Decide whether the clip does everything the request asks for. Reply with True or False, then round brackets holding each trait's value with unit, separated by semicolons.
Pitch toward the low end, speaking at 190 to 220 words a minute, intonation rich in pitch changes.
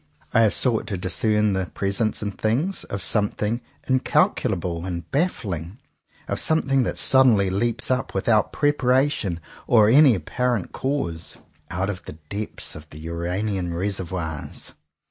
False (105 Hz; 145 wpm; 5.7 semitones)